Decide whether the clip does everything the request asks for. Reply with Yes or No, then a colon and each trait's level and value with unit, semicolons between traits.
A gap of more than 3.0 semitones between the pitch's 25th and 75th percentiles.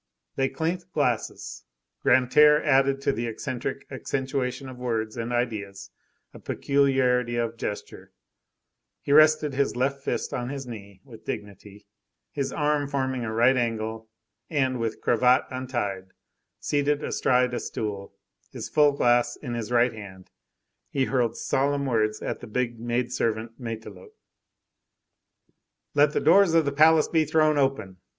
Yes: average, 3.7 semitones